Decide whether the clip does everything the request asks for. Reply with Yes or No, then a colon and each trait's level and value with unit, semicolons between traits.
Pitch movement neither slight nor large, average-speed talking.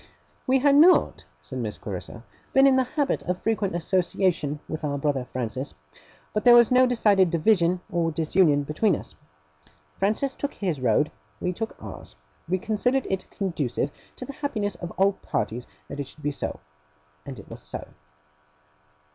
No: wide, 7.7 semitones; average, 165 wpm